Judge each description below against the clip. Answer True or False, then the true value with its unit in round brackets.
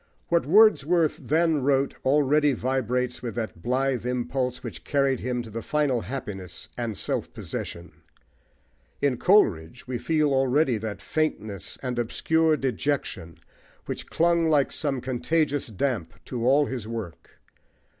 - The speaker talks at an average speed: False (130 wpm)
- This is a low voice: True (130 Hz)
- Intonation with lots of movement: False (4.2 semitones)